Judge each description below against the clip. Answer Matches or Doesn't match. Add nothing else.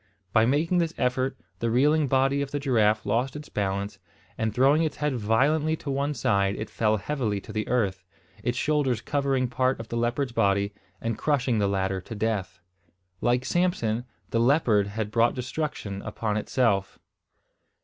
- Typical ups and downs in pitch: Matches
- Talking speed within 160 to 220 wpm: Matches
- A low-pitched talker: Matches